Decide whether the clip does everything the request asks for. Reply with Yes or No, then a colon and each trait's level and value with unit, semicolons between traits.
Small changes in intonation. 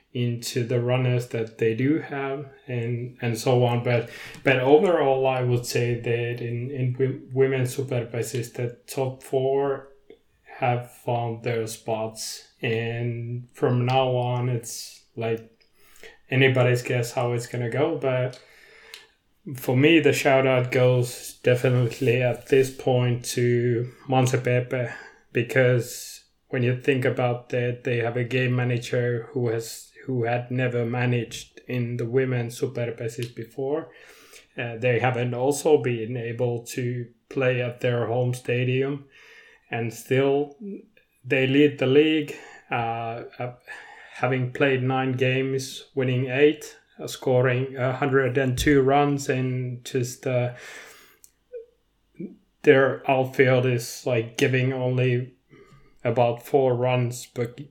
Yes: narrow, 1.8 semitones